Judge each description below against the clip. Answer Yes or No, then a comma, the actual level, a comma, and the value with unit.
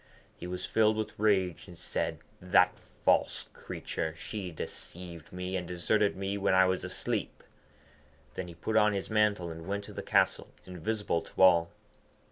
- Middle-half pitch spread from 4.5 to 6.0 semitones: No, average, 2.7 semitones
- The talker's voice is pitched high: No, very low, 95 Hz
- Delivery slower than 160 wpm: No, average, 165 wpm